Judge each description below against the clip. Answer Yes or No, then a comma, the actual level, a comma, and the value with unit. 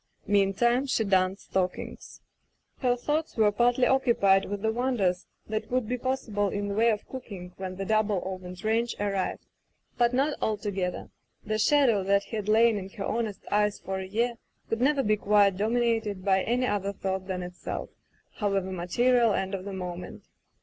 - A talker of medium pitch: No, high, 210 Hz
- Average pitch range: Yes, average, 3.6 semitones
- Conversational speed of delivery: Yes, average, 170 wpm